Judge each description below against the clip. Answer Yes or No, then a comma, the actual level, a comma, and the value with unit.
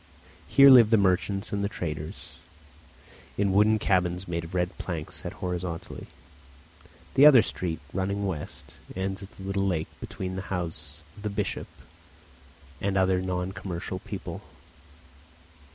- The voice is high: No, very low, 95 Hz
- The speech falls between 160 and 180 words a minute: No, slow, 135 wpm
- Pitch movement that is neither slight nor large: No, narrow, 2.1 semitones